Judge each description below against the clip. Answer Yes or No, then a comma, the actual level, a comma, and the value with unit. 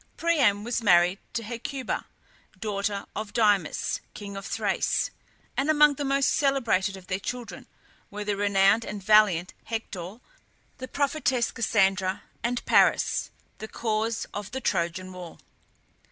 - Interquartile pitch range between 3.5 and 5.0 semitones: Yes, average, 3.8 semitones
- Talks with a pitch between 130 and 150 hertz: No, high, 210 Hz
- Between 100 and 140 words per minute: Yes, slow, 135 wpm